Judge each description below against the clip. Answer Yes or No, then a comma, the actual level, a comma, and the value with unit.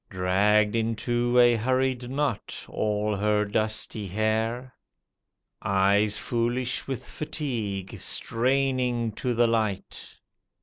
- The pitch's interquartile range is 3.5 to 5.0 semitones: No, average, 2.8 semitones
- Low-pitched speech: Yes, low, 115 Hz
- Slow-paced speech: Yes, slow, 95 wpm